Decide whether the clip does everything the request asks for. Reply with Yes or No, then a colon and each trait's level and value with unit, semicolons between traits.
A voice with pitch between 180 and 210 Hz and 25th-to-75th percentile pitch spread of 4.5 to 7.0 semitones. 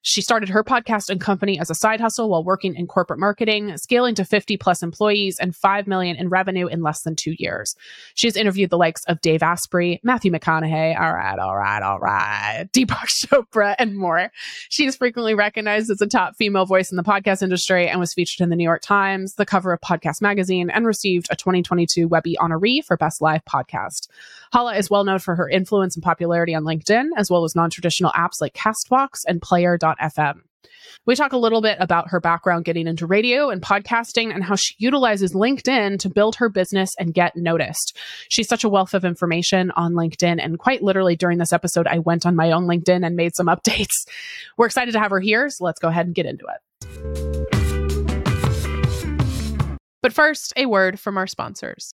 No: medium, 185 Hz; average, 4.0 semitones